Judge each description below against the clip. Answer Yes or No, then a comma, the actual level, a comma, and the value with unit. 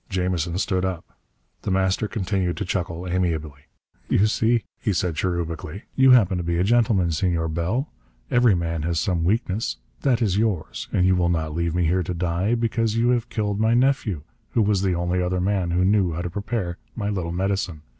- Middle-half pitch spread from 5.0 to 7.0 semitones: No, average, 3.6 semitones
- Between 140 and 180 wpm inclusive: No, average, 195 wpm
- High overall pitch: No, very low, 95 Hz